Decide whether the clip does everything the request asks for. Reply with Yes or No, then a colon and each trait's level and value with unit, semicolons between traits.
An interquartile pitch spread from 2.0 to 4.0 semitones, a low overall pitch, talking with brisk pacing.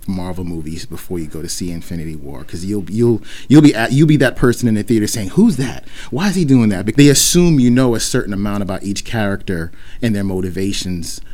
No: wide, 5.4 semitones; low, 100 Hz; fast, 240 wpm